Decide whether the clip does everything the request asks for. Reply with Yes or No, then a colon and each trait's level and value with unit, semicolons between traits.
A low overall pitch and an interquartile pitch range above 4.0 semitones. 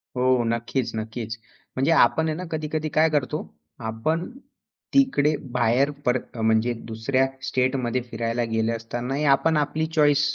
Yes: low, 130 Hz; average, 4.6 semitones